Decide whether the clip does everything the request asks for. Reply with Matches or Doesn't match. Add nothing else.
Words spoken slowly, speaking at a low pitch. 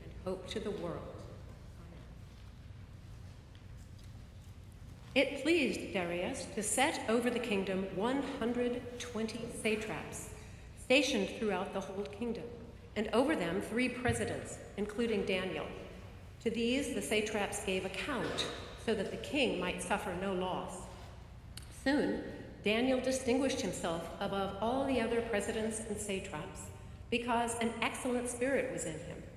Doesn't match